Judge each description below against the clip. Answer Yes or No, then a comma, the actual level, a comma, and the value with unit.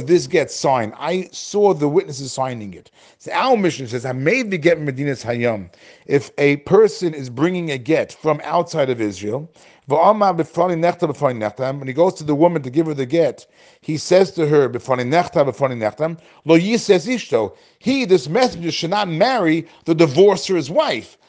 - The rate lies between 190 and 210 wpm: No, average, 160 wpm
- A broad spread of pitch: No, average, 4.8 semitones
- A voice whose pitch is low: No, medium, 160 Hz